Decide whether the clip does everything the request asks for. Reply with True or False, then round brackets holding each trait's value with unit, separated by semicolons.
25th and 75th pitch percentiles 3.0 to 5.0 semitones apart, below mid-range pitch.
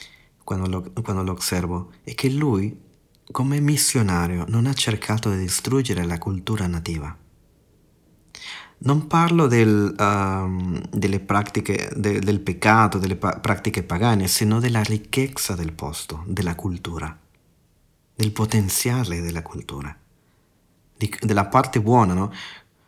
True (3.9 semitones; 100 Hz)